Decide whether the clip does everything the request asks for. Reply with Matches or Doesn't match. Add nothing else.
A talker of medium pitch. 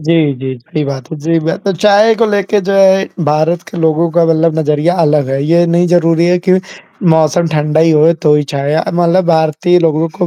Matches